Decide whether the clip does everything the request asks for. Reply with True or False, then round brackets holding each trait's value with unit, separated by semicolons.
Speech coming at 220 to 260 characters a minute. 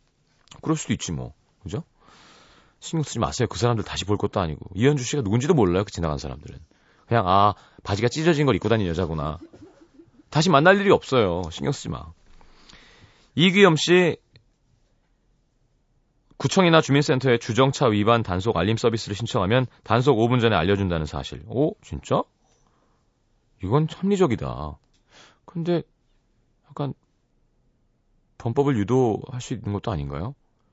False (295 characters per minute)